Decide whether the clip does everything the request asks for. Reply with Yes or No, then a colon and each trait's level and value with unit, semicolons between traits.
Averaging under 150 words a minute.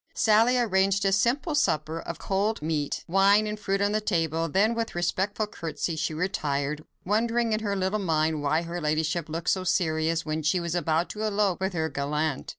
No: average, 195 wpm